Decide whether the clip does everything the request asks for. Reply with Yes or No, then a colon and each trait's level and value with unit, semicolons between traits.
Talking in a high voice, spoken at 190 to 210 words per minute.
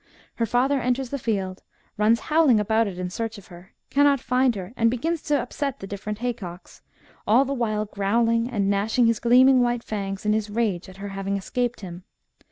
Yes: high, 225 Hz; average, 195 wpm